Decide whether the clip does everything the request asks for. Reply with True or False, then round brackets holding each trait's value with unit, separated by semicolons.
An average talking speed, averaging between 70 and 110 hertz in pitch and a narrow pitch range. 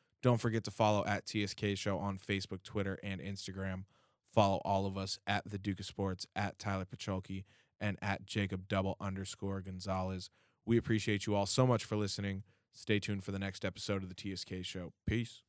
True (190 wpm; 100 Hz; 1.6 semitones)